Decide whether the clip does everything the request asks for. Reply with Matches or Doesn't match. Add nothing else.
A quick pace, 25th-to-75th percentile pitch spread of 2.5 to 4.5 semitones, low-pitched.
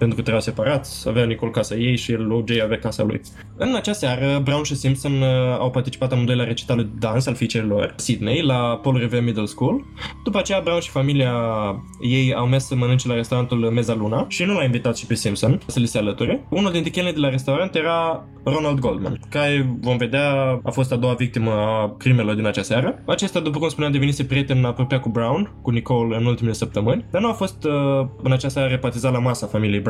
Matches